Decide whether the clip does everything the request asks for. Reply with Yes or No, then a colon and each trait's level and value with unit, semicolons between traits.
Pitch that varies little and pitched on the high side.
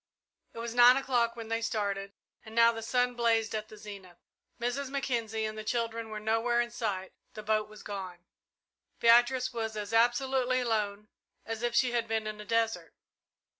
Yes: narrow, 2.0 semitones; high, 225 Hz